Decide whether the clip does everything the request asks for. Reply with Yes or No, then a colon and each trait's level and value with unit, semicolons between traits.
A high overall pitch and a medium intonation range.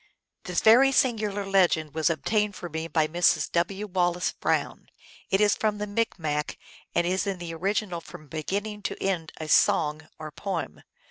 No: medium, 180 Hz; average, 4.3 semitones